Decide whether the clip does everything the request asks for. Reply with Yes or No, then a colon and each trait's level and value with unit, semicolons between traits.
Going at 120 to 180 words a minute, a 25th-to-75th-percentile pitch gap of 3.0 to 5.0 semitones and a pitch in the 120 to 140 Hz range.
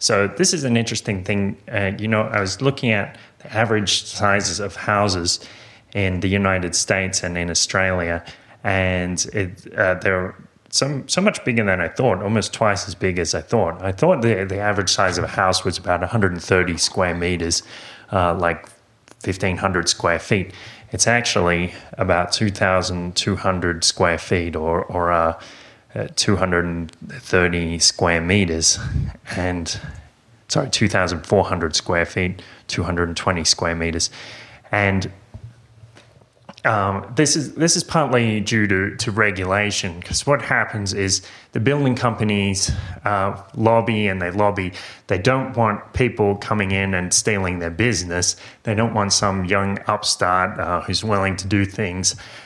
No: average, 150 wpm; average, 3.7 semitones; low, 100 Hz